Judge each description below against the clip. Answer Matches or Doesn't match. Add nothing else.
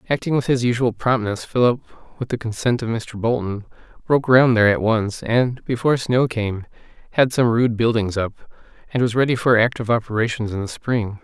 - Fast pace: Doesn't match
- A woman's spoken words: Doesn't match